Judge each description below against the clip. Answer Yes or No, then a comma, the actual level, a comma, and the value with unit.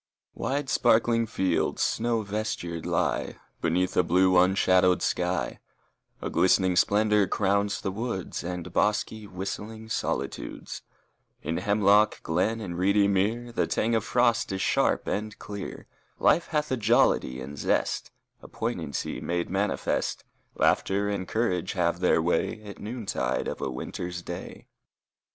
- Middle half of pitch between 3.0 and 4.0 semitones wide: Yes, average, 3.3 semitones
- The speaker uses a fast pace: No, slow, 135 wpm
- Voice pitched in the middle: No, low, 100 Hz